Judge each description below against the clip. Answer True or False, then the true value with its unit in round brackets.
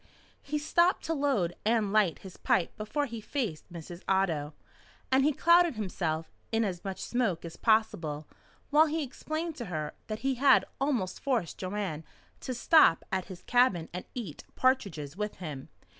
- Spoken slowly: False (165 wpm)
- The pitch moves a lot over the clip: True (7.5 semitones)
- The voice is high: True (215 Hz)